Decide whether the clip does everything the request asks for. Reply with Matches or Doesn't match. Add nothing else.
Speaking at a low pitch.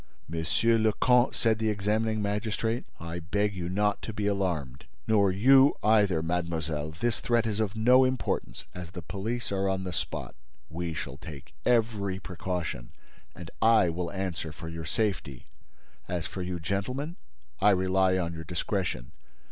Matches